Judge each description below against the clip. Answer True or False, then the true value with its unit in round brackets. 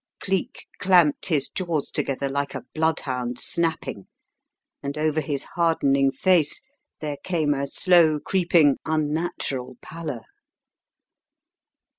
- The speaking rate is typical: False (110 wpm)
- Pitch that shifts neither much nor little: True (3.3 semitones)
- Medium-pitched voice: True (155 Hz)